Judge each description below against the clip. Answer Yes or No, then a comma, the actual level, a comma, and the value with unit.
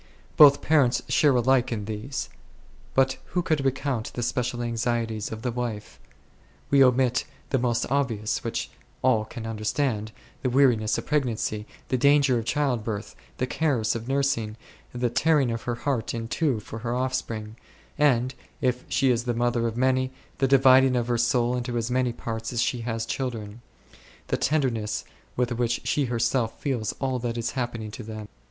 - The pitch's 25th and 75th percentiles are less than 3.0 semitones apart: Yes, narrow, 2.6 semitones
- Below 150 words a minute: No, average, 170 wpm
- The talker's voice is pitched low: Yes, low, 120 Hz